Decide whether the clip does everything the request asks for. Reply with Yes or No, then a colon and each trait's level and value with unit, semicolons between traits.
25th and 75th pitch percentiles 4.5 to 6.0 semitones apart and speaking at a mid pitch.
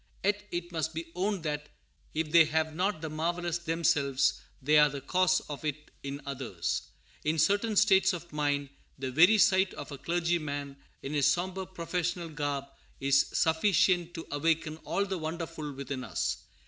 No: average, 3.3 semitones; medium, 160 Hz